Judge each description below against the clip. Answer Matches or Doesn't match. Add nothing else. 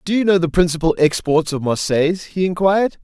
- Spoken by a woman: Doesn't match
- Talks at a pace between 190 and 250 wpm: Matches